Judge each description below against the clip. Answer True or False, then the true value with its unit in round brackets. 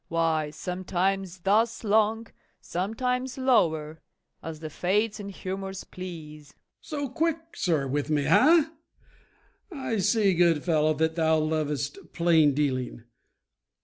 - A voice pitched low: False (175 Hz)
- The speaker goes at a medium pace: False (115 wpm)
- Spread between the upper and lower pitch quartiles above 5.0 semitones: True (5.6 semitones)